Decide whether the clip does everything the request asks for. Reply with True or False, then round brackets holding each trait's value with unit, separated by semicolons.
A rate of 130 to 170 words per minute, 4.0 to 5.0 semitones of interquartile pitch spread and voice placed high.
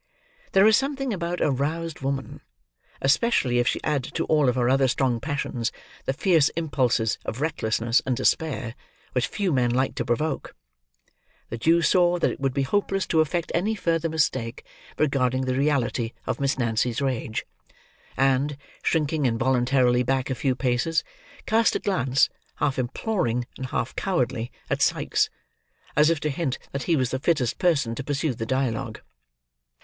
False (165 wpm; 4.5 semitones; 135 Hz)